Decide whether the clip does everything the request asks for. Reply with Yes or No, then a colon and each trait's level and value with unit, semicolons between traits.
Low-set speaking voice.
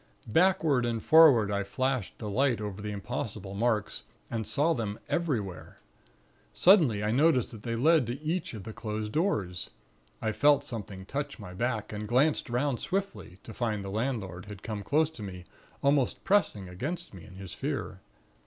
Yes: low, 115 Hz